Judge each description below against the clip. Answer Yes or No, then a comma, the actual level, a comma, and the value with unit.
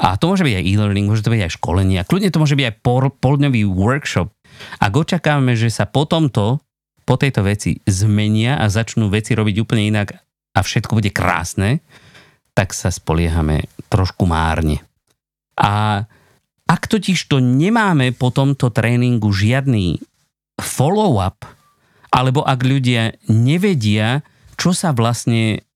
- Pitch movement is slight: No, average, 4.8 semitones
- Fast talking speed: No, average, 145 wpm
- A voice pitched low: Yes, low, 115 Hz